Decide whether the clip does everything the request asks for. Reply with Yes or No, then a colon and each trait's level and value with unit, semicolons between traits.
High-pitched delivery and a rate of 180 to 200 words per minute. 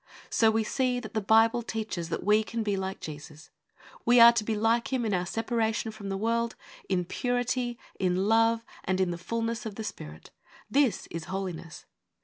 Yes: high, 220 Hz; average, 190 wpm